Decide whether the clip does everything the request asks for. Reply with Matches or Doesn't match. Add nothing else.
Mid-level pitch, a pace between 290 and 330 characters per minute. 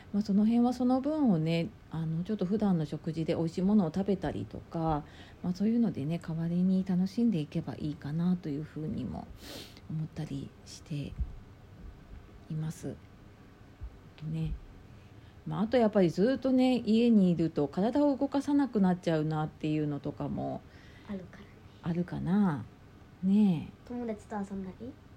Matches